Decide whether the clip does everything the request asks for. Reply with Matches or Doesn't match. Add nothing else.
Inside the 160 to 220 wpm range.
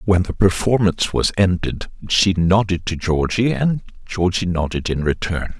Doesn't match